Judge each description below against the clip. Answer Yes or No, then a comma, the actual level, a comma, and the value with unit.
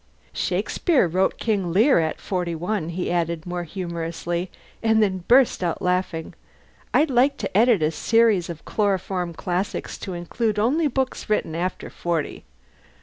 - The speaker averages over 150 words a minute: No, average, 145 wpm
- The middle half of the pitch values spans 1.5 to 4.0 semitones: No, average, 4.4 semitones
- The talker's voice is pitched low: No, medium, 185 Hz